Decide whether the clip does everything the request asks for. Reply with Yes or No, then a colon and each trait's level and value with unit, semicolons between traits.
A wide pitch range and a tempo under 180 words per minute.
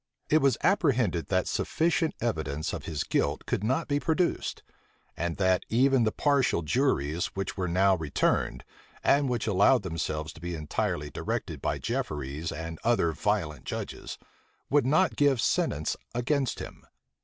Yes: wide, 8.9 semitones; average, 150 wpm